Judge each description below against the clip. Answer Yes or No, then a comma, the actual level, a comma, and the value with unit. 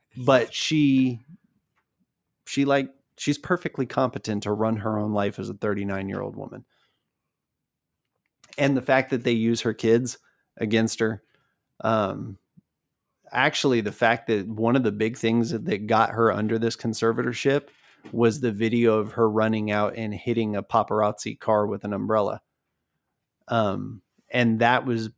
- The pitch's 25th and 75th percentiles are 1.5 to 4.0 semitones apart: Yes, average, 3.2 semitones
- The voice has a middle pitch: No, low, 115 Hz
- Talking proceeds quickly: No, average, 145 wpm